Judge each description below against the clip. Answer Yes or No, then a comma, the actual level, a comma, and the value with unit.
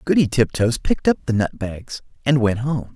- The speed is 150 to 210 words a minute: Yes, fast, 205 wpm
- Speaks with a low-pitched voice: Yes, low, 120 Hz